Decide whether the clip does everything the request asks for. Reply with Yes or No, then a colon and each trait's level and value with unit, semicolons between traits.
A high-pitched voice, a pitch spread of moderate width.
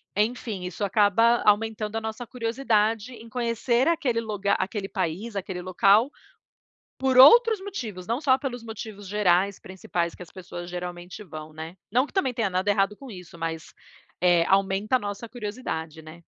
Yes: high, 210 Hz; average, 4.3 semitones